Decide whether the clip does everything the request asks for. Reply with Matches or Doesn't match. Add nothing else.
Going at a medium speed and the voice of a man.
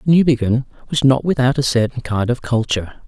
Matches